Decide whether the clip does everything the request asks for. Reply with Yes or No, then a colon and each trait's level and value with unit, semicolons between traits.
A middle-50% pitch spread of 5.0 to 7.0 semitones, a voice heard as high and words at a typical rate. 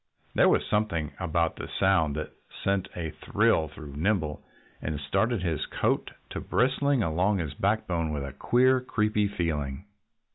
No: wide, 5.5 semitones; very low, 85 Hz; average, 150 wpm